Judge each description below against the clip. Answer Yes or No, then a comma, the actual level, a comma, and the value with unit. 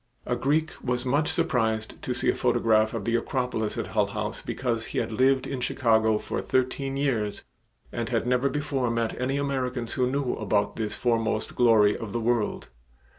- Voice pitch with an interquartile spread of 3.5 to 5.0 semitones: No, average, 2.8 semitones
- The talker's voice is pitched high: No, low, 120 Hz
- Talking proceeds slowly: No, average, 180 wpm